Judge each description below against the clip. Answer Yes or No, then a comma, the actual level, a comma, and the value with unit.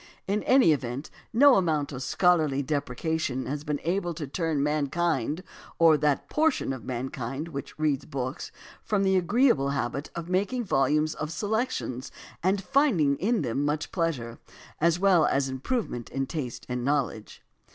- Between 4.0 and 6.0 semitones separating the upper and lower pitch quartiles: Yes, average, 5.1 semitones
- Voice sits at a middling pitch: Yes, medium, 150 Hz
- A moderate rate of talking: Yes, average, 150 wpm